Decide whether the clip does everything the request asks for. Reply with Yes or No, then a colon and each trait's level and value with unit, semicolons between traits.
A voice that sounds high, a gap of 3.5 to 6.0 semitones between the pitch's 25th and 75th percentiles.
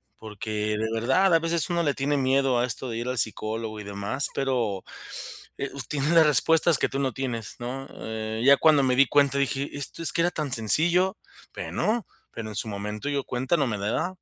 No: low, 135 Hz; average, 4.7 semitones